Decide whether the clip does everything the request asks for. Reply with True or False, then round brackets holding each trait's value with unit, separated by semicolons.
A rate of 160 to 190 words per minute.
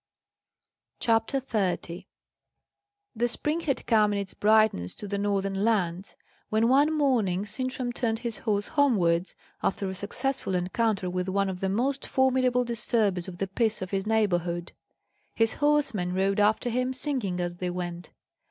False (150 wpm)